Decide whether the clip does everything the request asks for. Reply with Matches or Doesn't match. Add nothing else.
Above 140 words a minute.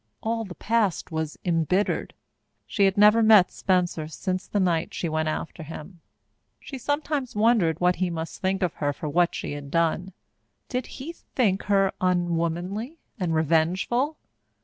Matches